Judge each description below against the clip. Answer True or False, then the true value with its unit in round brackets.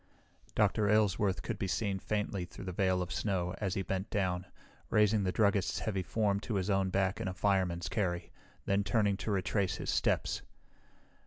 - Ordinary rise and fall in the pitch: False (1.9 semitones)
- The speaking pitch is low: True (100 Hz)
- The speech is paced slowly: False (180 wpm)